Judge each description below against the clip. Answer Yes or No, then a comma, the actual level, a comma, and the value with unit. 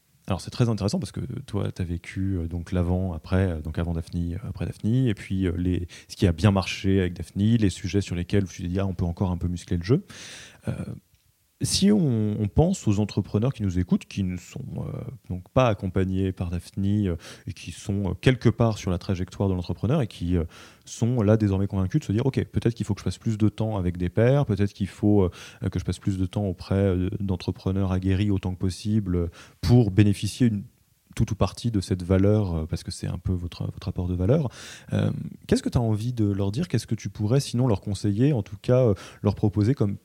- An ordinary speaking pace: No, fast, 235 wpm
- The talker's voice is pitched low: Yes, low, 100 Hz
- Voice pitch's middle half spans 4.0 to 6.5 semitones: No, average, 3.4 semitones